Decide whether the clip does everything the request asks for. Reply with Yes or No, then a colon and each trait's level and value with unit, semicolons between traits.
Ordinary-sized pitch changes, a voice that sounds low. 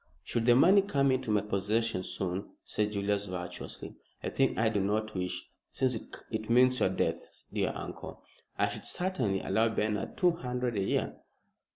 Yes: average, 4.2 semitones; low, 110 Hz